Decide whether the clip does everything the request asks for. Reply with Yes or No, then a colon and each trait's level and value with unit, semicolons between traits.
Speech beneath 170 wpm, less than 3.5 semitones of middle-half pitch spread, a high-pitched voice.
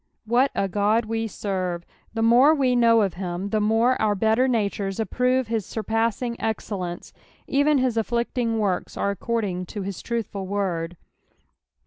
Yes: average, 160 wpm; average, 3.1 semitones; high, 220 Hz